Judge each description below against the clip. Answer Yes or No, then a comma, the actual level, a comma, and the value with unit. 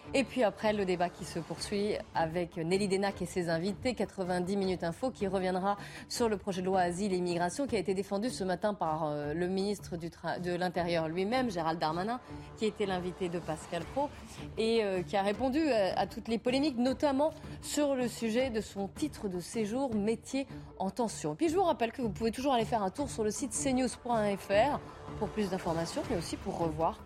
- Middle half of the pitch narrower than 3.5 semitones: No, average, 4.7 semitones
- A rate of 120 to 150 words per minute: No, average, 205 wpm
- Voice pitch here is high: Yes, high, 200 Hz